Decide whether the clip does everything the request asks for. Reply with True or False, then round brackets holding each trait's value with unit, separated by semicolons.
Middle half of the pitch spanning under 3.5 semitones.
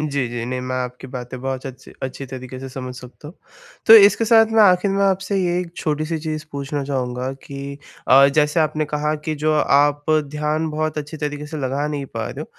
True (2.9 semitones)